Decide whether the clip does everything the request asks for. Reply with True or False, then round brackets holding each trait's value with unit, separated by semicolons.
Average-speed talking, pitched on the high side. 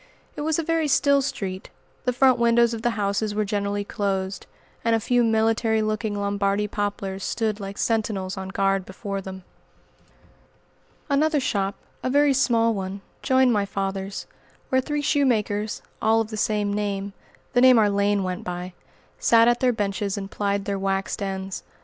True (170 wpm; 210 Hz)